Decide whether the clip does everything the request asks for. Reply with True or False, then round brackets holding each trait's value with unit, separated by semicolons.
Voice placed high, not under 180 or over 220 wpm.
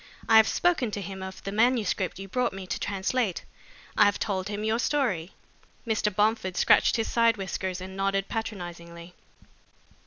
False (200 Hz; 165 wpm)